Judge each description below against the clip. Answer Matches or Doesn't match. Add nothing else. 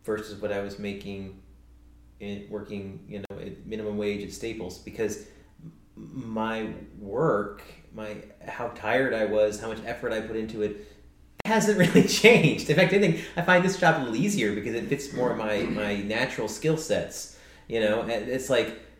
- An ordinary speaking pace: Matches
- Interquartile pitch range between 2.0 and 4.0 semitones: Doesn't match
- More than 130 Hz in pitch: Doesn't match